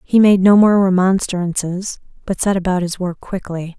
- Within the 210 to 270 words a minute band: No, average, 175 wpm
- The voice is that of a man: No, female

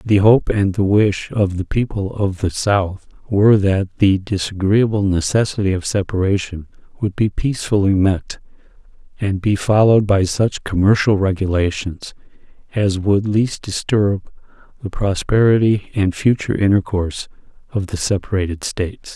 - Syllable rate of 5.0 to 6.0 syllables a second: No, 4.7 syllables/s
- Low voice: Yes, low, 100 Hz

